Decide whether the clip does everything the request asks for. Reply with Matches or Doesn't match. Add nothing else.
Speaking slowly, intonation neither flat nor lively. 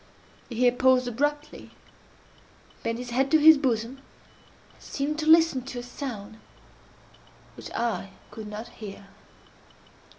Matches